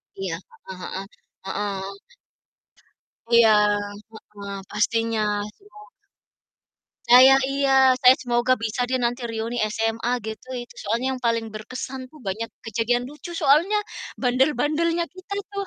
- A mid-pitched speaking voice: No, high, 240 Hz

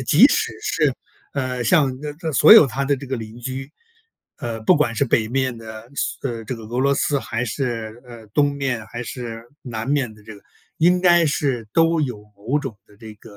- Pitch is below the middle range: Yes, low, 125 Hz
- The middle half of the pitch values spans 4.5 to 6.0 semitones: No, average, 3.7 semitones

